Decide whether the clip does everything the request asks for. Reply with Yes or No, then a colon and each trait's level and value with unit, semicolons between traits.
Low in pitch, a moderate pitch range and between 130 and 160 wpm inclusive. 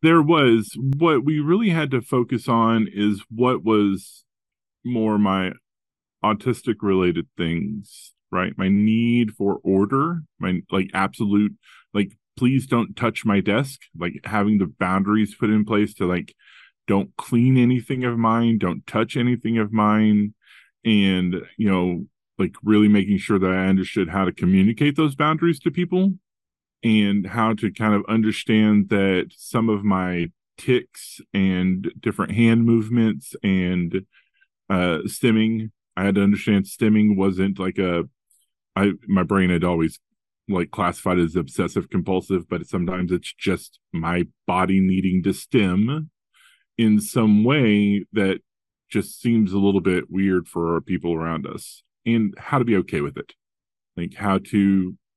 Yes: low, 105 Hz; average, 3.5 semitones; average, 150 wpm